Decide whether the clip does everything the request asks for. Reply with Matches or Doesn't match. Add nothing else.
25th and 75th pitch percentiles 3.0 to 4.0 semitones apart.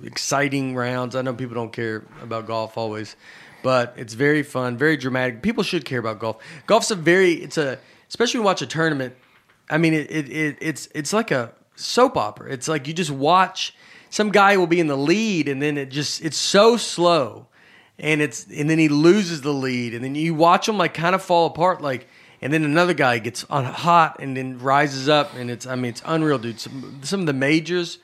Doesn't match